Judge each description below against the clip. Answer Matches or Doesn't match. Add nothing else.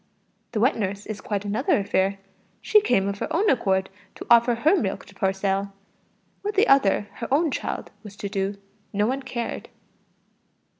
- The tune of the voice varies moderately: Matches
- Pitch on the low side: Doesn't match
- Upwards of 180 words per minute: Doesn't match